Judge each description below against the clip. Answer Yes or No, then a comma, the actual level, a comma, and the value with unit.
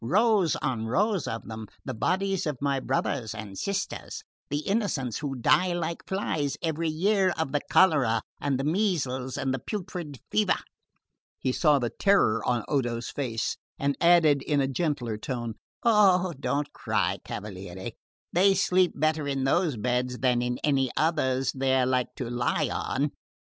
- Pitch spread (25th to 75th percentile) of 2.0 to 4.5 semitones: No, wide, 5.6 semitones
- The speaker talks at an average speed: Yes, average, 160 wpm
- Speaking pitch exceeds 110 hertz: Yes, medium, 140 Hz